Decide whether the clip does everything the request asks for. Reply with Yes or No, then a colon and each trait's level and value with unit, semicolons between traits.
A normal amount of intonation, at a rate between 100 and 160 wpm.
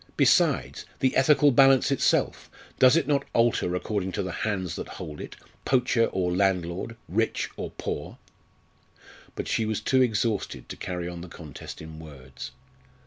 No: wide, 6.1 semitones; average, 155 wpm